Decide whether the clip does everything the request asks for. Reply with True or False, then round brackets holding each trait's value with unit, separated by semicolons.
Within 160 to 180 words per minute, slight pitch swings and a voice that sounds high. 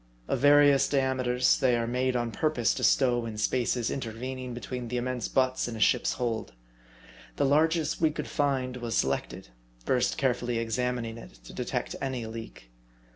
False (165 wpm; 2.1 semitones; 125 Hz)